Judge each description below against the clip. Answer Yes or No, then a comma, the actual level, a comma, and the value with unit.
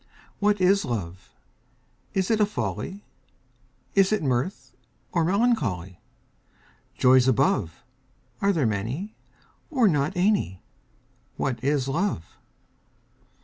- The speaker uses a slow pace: Yes, slow, 105 wpm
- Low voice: No, medium, 155 Hz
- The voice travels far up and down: Yes, wide, 9.0 semitones